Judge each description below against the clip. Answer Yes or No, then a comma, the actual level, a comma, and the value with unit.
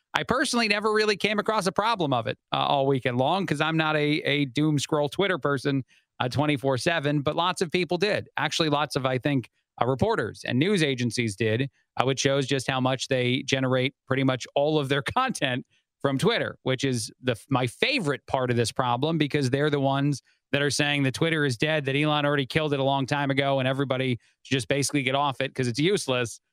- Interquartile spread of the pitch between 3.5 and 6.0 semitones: No, average, 2.7 semitones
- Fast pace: Yes, fast, 220 wpm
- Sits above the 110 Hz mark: Yes, medium, 140 Hz